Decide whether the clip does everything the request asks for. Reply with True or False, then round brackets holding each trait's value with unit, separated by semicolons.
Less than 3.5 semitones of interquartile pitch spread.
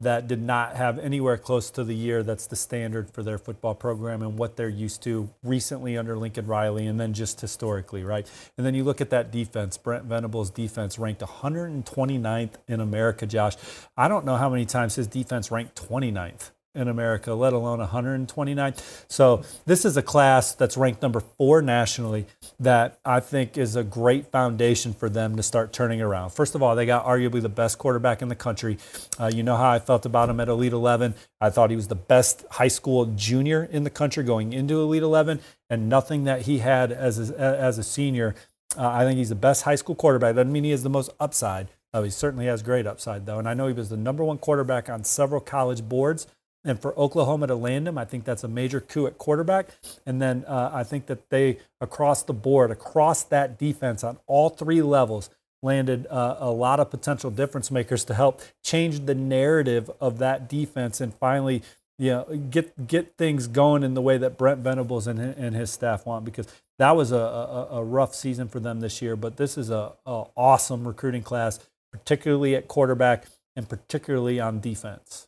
True (2.9 semitones)